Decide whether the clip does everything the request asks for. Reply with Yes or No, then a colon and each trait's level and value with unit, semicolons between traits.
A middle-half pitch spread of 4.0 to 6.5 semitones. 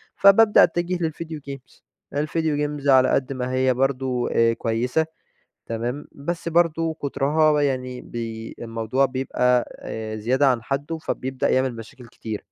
No: average, 3.5 semitones